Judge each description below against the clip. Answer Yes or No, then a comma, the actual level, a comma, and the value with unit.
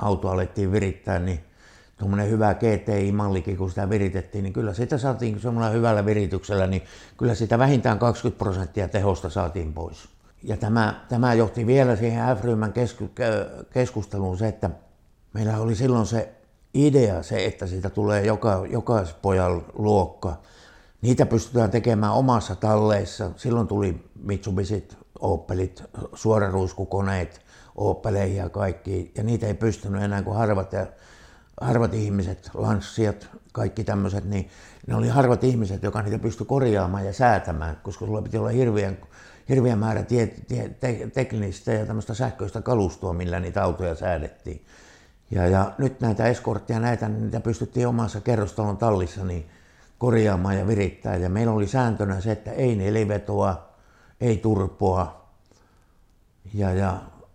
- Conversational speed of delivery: Yes, average, 140 wpm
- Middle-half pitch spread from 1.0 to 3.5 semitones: Yes, average, 3.1 semitones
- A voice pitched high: No, low, 105 Hz